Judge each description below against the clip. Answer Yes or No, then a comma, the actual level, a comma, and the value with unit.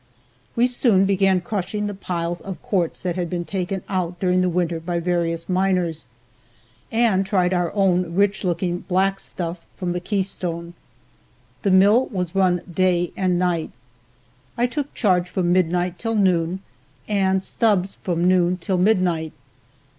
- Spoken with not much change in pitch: Yes, narrow, 1.8 semitones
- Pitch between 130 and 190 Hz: Yes, medium, 185 Hz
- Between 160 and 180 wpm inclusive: No, average, 150 wpm